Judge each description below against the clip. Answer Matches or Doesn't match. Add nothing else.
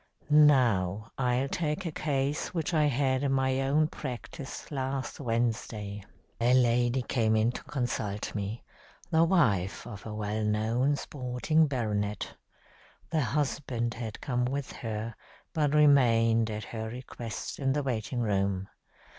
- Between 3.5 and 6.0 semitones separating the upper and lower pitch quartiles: Matches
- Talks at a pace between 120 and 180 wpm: Matches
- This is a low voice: Matches